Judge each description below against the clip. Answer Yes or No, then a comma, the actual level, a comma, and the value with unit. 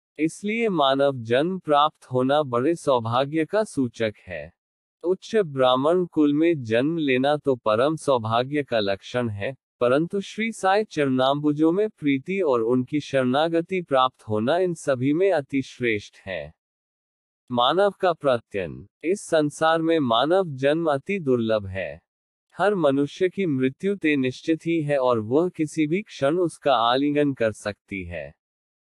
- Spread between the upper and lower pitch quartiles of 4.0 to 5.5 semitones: Yes, average, 4.7 semitones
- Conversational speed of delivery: Yes, average, 140 wpm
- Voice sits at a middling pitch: Yes, medium, 145 Hz